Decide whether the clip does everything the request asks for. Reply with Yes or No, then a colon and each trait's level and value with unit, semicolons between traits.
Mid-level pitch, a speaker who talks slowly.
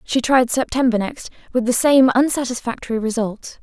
No: high, 245 Hz; slow, 130 wpm